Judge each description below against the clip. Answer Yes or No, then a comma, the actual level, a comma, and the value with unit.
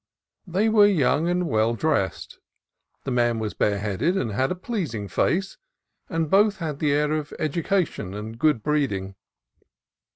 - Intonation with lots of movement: Yes, wide, 8.0 semitones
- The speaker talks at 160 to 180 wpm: No, average, 150 wpm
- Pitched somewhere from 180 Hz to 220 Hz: No, medium, 150 Hz